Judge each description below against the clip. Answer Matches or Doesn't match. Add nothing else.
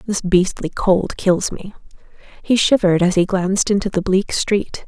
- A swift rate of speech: Doesn't match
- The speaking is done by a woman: Matches